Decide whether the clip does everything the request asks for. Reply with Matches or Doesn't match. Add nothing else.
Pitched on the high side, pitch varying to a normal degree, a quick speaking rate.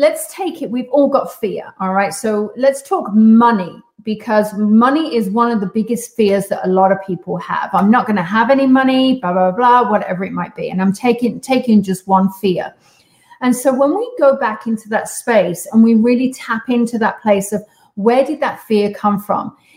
Matches